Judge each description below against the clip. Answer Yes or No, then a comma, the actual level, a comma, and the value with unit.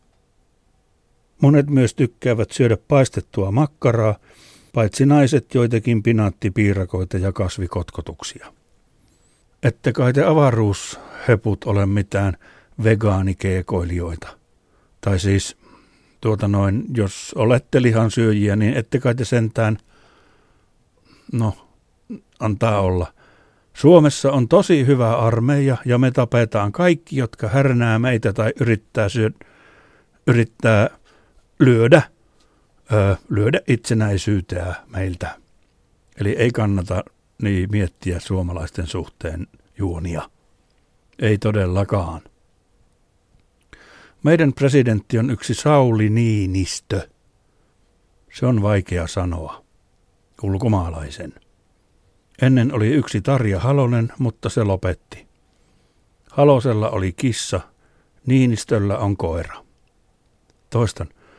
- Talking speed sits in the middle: No, slow, 90 wpm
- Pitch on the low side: Yes, low, 110 Hz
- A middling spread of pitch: Yes, average, 4.1 semitones